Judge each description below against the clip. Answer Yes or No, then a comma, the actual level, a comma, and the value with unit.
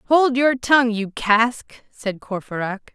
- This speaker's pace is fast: No, average, 145 wpm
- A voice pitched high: Yes, high, 235 Hz